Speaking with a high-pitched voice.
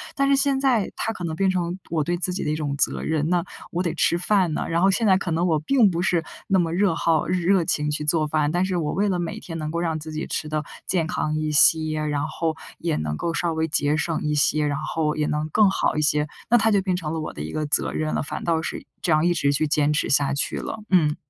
No: medium, 165 Hz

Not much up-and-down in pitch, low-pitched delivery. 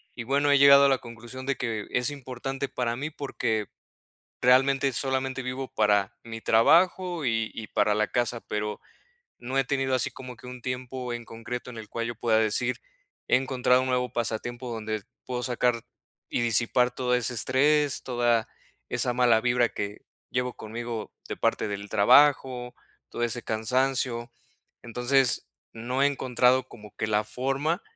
Yes: narrow, 2.3 semitones; low, 125 Hz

